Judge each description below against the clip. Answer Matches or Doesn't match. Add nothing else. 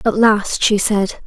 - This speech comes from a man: Doesn't match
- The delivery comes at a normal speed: Matches